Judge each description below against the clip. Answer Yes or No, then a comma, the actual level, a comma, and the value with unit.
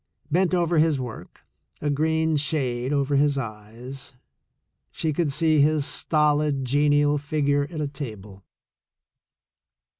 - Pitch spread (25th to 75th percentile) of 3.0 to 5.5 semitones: No, narrow, 2.4 semitones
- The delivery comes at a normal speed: No, slow, 120 wpm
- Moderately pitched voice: Yes, medium, 145 Hz